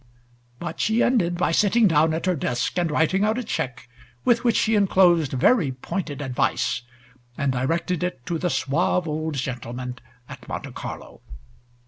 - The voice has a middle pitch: Yes, medium, 165 Hz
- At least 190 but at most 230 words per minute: No, average, 160 wpm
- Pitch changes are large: Yes, wide, 5.8 semitones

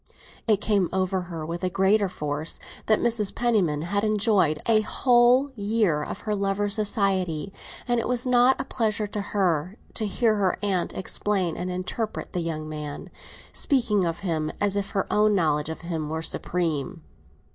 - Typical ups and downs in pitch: Yes, average, 4.3 semitones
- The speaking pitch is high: Yes, high, 195 Hz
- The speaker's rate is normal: Yes, average, 170 wpm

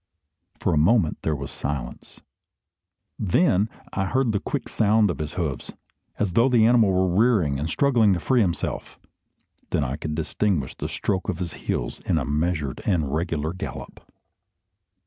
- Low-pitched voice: Yes, very low, 90 Hz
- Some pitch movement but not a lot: No, wide, 5.7 semitones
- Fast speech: No, average, 165 wpm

